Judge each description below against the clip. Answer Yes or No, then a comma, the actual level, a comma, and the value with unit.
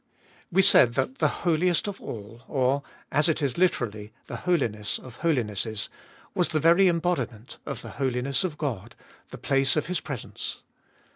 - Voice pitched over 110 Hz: Yes, medium, 140 Hz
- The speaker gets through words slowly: No, average, 160 wpm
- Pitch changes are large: Yes, wide, 6.3 semitones